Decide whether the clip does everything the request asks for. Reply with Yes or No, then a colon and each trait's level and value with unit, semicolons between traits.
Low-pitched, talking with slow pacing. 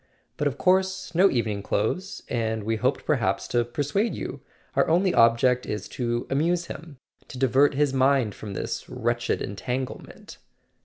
No: low, 130 Hz; average, 150 wpm